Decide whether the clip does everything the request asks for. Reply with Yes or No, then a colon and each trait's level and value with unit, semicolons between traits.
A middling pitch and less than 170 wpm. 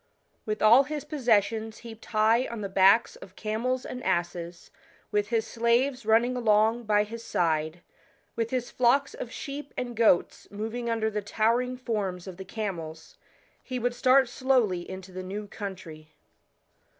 No: high, 220 Hz; average, 155 wpm